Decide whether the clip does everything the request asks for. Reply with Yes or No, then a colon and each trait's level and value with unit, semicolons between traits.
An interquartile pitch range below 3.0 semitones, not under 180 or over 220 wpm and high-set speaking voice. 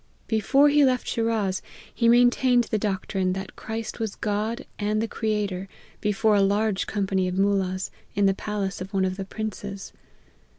No: narrow, 2.4 semitones; average, 165 wpm; high, 205 Hz